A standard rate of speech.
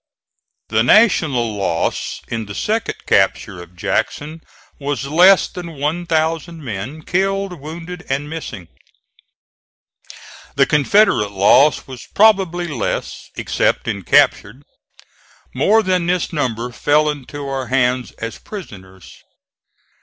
No: slow, 115 wpm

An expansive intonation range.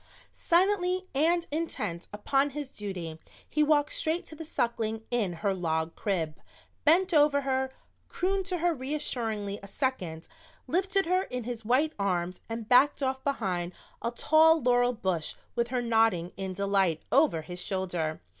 Yes: wide, 8.0 semitones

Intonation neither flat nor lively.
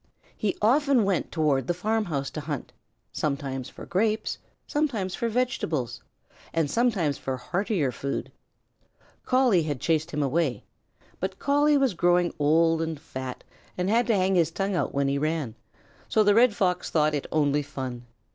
No: wide, 6.6 semitones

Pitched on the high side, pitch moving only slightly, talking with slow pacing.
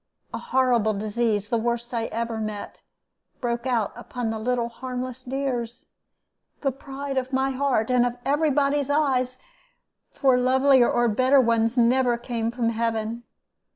No: high, 245 Hz; narrow, 2.3 semitones; average, 150 wpm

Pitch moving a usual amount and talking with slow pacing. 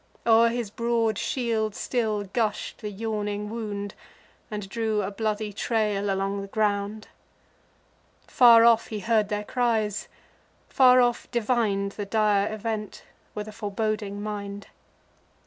No: narrow, 1.9 semitones; slow, 130 wpm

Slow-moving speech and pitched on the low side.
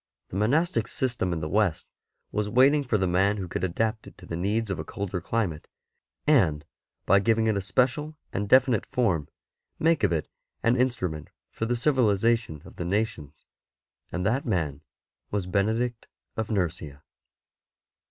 No: average, 160 wpm; low, 105 Hz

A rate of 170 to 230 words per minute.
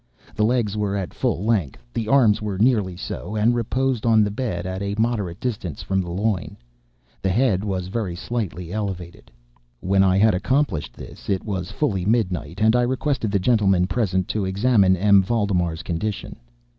Yes: average, 175 wpm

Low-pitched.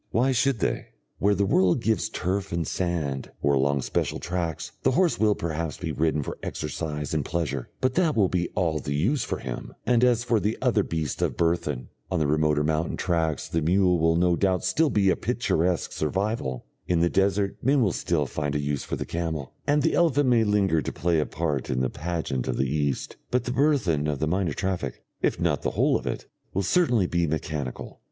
Yes: very low, 85 Hz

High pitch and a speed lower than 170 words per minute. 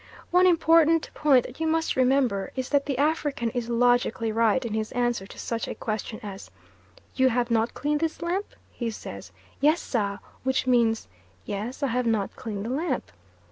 No: high, 245 Hz; average, 180 wpm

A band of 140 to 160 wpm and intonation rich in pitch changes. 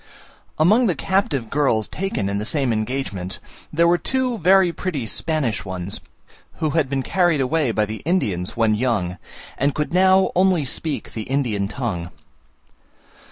Yes: average, 155 wpm; wide, 8.1 semitones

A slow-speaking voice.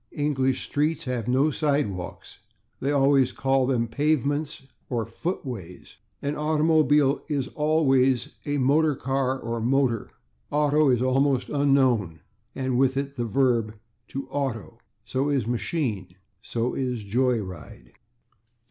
Yes: slow, 125 wpm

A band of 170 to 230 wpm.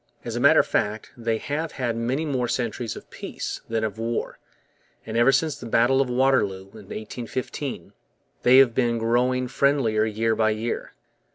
Yes: average, 175 wpm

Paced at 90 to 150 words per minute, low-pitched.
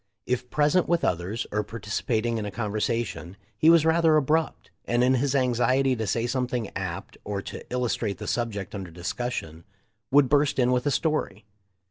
No: average, 175 wpm; low, 120 Hz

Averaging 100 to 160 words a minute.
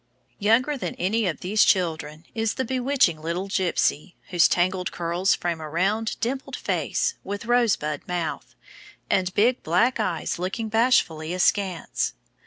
Yes: average, 140 wpm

